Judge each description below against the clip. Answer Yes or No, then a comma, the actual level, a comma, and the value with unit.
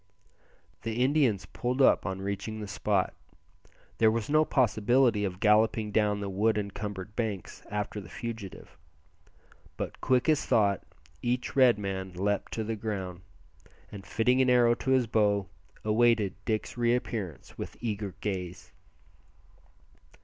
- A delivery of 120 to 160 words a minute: Yes, average, 140 wpm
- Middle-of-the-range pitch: No, low, 105 Hz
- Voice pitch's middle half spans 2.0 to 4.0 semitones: Yes, average, 3.0 semitones